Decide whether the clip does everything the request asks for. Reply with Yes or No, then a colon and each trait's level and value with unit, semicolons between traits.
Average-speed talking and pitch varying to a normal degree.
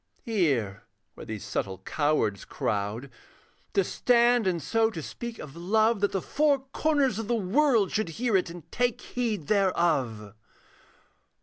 No: average, 145 wpm; wide, 7.9 semitones